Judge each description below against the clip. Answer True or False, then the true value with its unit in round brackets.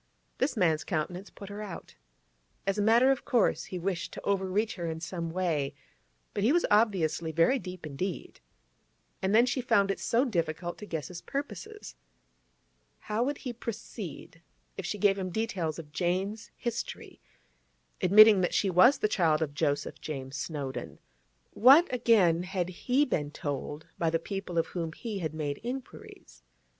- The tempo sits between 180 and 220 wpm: False (165 wpm)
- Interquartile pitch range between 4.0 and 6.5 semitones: True (4.9 semitones)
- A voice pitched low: False (185 Hz)